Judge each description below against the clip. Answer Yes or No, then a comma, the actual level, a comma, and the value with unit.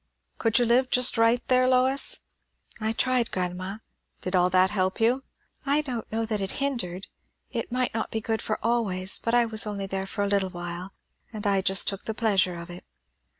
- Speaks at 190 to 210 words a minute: Yes, average, 200 wpm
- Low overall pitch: No, high, 220 Hz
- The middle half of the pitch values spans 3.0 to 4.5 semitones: Yes, average, 4.1 semitones